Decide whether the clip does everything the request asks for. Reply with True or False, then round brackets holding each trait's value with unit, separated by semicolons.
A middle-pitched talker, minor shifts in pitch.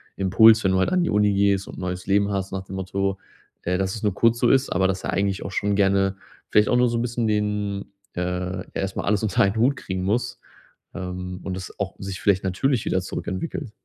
False (100 Hz; 2.2 semitones)